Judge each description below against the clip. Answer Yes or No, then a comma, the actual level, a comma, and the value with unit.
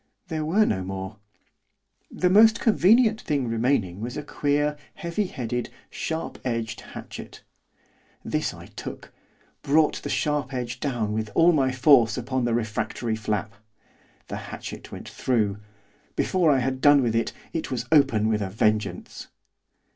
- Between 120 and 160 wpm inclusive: Yes, average, 145 wpm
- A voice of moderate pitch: No, low, 125 Hz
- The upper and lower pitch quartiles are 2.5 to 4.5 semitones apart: No, wide, 5.4 semitones